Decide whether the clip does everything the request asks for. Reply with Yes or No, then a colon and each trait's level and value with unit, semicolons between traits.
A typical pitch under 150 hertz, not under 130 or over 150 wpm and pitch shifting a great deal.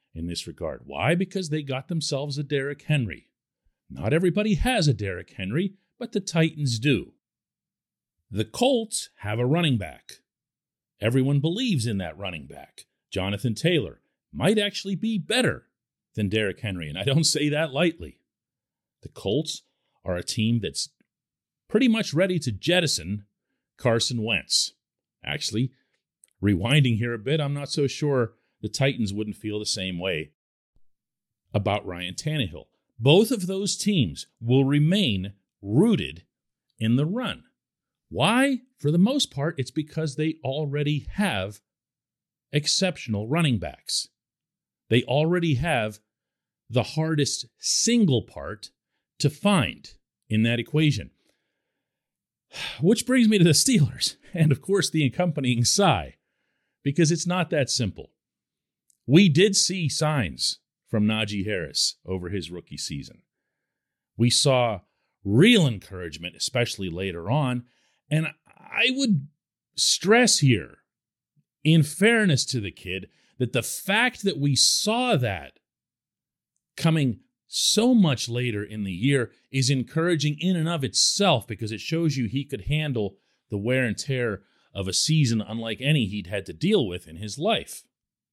Yes: medium, 140 Hz; average, 140 wpm; wide, 7.3 semitones